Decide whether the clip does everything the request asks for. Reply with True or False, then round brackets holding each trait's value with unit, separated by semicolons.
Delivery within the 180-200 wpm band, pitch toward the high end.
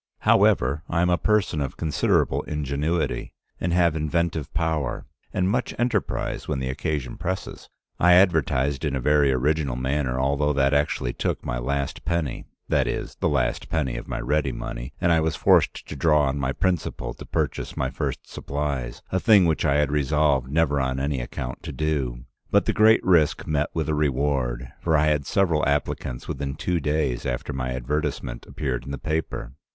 False (185 wpm; 75 Hz)